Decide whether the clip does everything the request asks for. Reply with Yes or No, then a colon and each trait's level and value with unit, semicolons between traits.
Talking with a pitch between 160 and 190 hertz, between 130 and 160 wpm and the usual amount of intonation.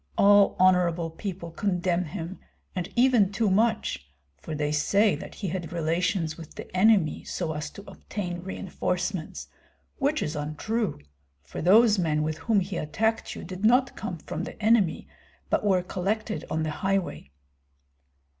Yes: medium, 185 Hz; average, 155 wpm; average, 4.0 semitones